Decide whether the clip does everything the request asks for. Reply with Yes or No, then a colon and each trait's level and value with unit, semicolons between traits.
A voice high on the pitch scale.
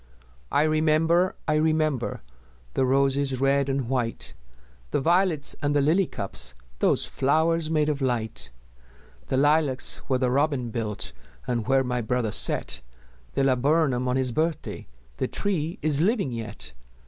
No: medium, 140 Hz